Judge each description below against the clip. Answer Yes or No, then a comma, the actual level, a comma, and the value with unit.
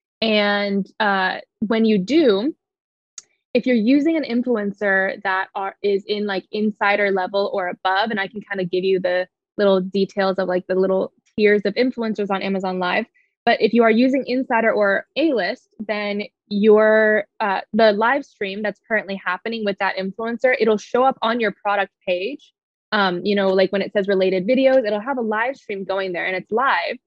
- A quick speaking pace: No, average, 190 wpm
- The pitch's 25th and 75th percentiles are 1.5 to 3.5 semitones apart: Yes, average, 2.8 semitones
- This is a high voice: Yes, high, 205 Hz